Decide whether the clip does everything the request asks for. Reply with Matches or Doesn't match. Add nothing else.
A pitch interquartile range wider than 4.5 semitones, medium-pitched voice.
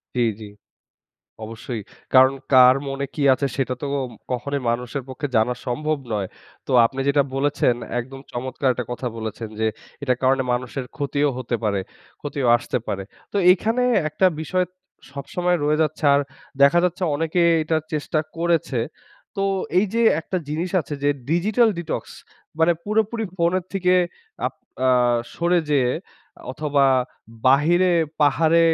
Matches